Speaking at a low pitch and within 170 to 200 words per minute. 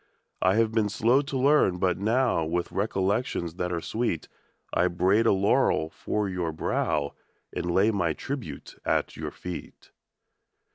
No: very low, 95 Hz; average, 155 wpm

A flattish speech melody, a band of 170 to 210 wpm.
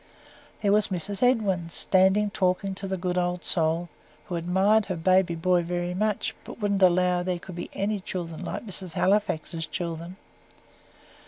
No: narrow, 2.3 semitones; average, 160 wpm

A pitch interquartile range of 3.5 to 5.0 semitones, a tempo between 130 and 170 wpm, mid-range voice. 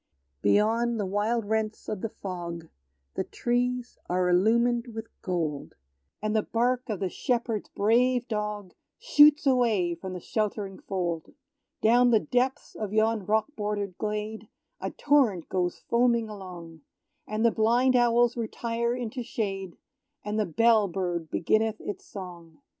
No: average, 3.8 semitones; average, 140 wpm; high, 215 Hz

